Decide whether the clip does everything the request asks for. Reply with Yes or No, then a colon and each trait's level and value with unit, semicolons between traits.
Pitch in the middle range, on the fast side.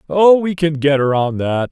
Yes: medium, 155 Hz; fast, 210 wpm